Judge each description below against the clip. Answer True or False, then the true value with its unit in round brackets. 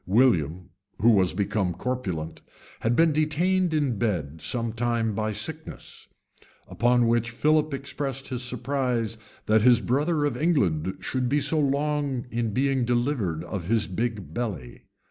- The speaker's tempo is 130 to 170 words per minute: True (145 wpm)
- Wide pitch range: False (5.0 semitones)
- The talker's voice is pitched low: True (120 Hz)